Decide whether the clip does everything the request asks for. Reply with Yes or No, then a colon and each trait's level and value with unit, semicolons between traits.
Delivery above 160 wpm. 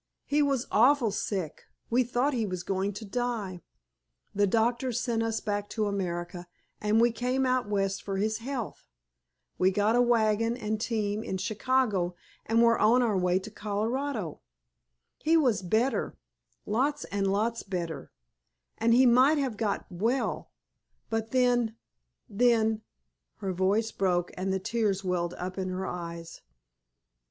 No: average, 145 wpm